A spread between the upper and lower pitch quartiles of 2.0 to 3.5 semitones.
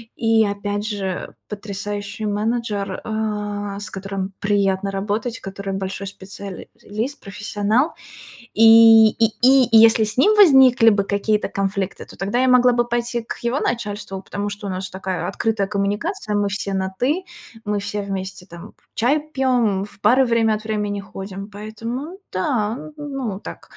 Yes: average, 2.8 semitones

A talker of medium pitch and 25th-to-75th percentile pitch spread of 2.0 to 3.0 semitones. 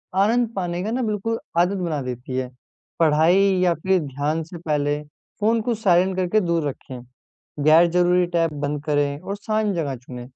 No: medium, 170 Hz; average, 4.9 semitones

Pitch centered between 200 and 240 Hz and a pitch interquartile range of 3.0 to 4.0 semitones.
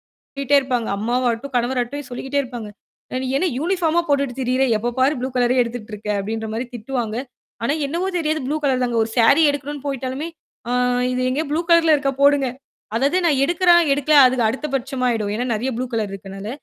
No: very high, 260 Hz; average, 3.3 semitones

